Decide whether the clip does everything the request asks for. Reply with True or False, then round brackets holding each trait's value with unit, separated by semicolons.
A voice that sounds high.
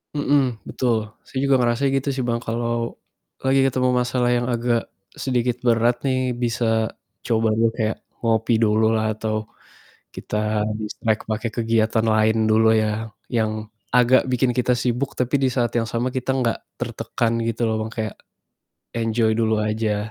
False (115 Hz)